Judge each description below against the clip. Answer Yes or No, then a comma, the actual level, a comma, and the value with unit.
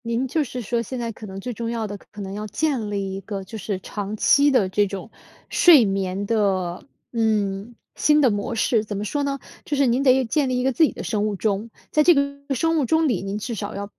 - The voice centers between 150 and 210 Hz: No, high, 225 Hz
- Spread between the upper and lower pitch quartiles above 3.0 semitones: Yes, average, 4.7 semitones